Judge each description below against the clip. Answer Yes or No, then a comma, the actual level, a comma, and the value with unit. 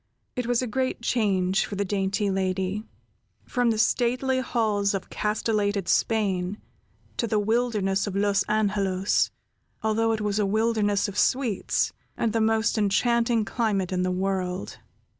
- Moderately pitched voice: No, high, 210 Hz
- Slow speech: No, average, 145 wpm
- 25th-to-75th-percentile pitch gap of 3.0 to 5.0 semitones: No, narrow, 2.6 semitones